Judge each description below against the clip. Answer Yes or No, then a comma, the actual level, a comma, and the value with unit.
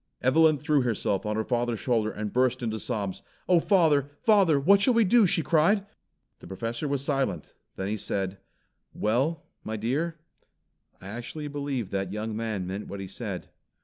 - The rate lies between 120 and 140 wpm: No, average, 175 wpm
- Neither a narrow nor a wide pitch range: No, wide, 6.4 semitones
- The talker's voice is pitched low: Yes, low, 120 Hz